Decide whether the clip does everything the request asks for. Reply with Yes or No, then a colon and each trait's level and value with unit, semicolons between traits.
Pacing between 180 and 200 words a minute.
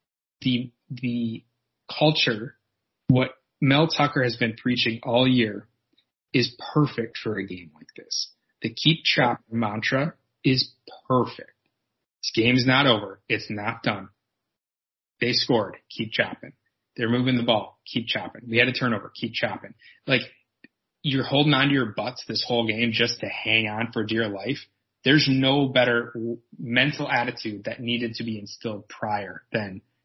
No: average, 155 wpm